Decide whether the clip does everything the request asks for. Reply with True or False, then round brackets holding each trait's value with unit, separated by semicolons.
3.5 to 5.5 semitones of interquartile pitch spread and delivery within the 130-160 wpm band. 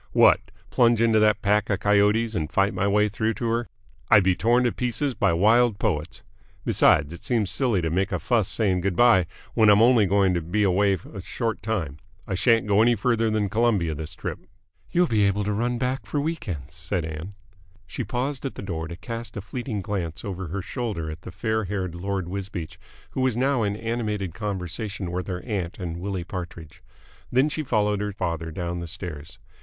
False (4.3 semitones; 205 wpm)